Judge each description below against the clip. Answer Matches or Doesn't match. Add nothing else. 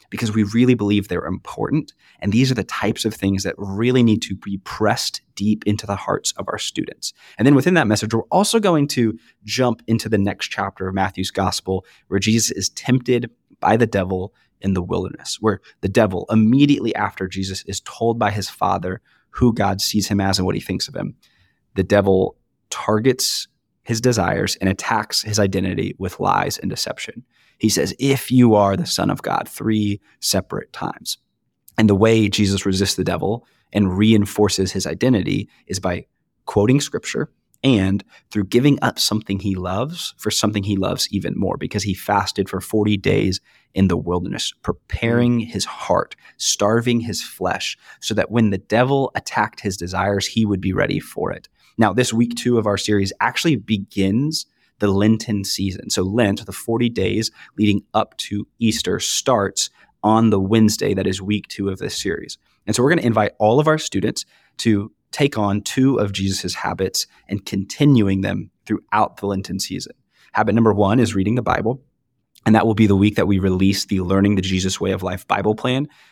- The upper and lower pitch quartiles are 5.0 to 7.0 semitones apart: Doesn't match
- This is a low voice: Matches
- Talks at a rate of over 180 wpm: Matches